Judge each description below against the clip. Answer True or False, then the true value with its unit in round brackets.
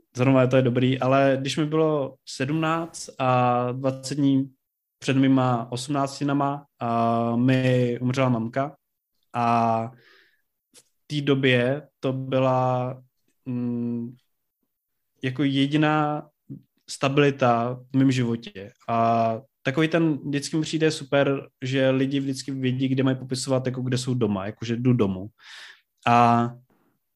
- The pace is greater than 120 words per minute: False (115 wpm)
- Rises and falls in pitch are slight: True (2.3 semitones)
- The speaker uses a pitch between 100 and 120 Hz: False (130 Hz)